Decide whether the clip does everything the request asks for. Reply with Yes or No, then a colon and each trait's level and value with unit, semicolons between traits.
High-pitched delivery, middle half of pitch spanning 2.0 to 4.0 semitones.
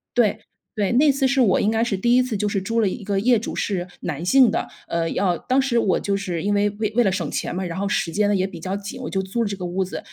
Yes: high, 205 Hz; average, 3.7 semitones